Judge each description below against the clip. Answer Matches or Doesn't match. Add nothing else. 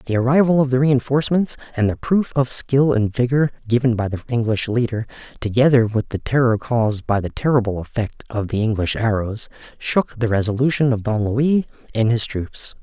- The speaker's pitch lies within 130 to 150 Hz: Doesn't match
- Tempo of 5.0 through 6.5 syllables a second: Matches